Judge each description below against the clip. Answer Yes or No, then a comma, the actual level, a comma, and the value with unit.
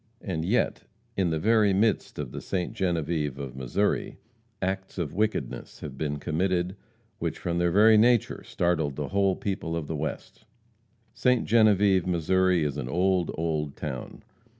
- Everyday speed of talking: Yes, average, 155 wpm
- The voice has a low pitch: Yes, very low, 90 Hz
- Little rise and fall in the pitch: No, average, 4.2 semitones